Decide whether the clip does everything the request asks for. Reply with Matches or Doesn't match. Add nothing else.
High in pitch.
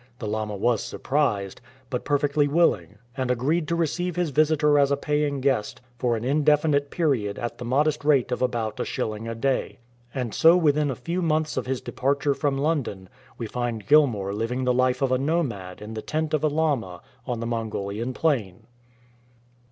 Doesn't match